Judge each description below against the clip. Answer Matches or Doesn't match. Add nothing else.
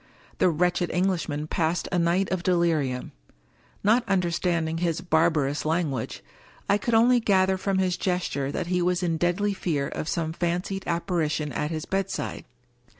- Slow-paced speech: Doesn't match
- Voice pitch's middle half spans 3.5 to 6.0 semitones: Doesn't match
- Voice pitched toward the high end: Doesn't match